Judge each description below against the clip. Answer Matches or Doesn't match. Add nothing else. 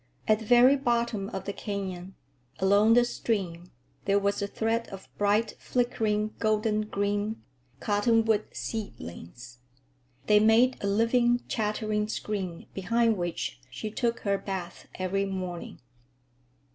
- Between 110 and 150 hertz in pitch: Doesn't match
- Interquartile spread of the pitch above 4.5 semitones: Doesn't match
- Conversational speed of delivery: Doesn't match